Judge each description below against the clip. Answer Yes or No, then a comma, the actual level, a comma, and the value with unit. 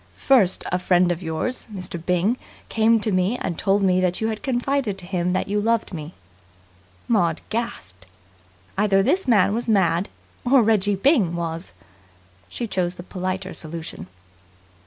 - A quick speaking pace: No, average, 155 wpm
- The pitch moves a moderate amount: Yes, average, 4.1 semitones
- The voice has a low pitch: No, high, 190 Hz